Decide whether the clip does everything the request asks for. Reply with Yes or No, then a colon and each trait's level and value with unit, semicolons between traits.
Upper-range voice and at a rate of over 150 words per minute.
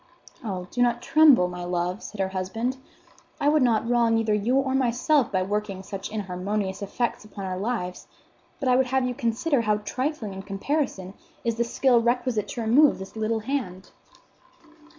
Yes: high, 225 Hz; average, 175 wpm